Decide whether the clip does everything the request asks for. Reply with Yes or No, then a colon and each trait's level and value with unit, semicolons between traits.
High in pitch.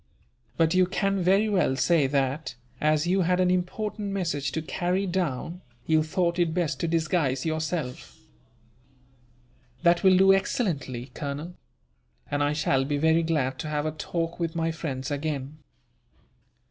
No: medium, 160 Hz